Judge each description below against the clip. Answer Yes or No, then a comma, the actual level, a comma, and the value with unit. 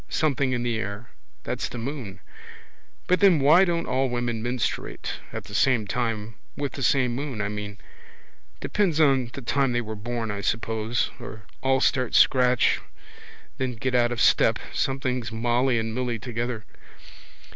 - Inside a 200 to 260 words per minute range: No, average, 160 wpm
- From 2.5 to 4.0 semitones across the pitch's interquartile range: Yes, average, 2.9 semitones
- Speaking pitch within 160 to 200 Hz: No, low, 120 Hz